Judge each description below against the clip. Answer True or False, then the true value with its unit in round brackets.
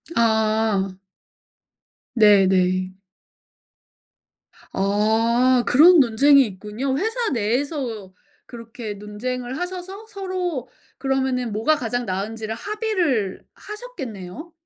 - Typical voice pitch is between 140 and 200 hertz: False (240 Hz)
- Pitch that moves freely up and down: True (6.0 semitones)